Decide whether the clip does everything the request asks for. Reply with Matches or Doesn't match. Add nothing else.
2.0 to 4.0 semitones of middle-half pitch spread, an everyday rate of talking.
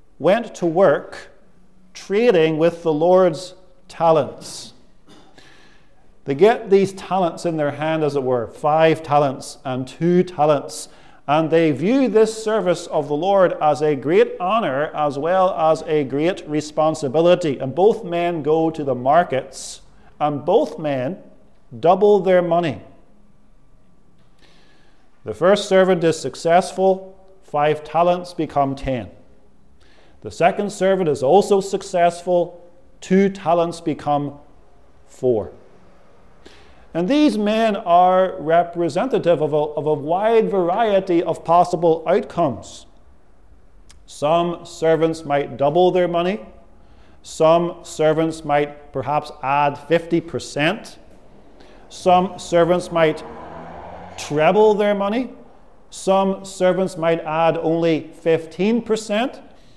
Doesn't match